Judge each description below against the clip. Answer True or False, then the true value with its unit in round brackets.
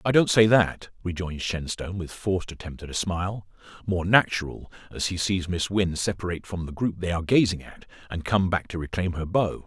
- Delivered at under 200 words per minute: False (205 wpm)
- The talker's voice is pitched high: False (90 Hz)